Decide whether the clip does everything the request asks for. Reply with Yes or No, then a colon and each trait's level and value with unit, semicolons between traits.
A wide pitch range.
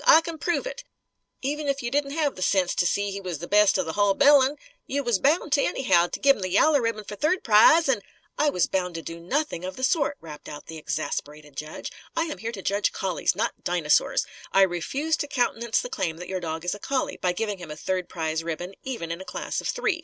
Yes: wide, 8.2 semitones